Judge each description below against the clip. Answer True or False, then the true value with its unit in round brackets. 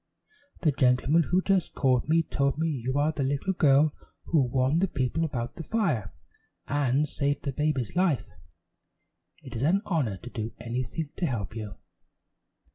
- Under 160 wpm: False (165 wpm)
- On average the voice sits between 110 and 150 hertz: True (140 Hz)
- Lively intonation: False (4.4 semitones)